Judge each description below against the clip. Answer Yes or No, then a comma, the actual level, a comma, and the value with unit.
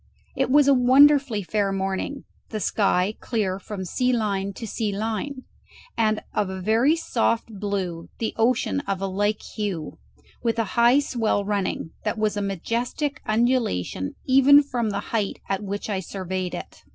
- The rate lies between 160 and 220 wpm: Yes, average, 165 wpm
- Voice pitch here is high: Yes, high, 215 Hz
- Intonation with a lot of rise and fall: No, average, 4.1 semitones